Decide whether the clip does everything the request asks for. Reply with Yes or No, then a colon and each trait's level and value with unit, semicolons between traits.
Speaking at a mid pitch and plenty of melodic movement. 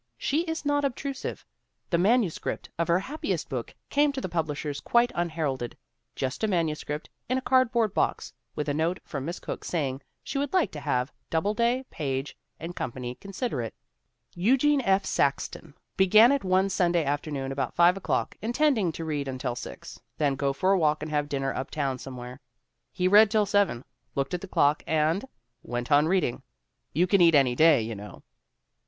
Yes: medium, 165 Hz; wide, 6.9 semitones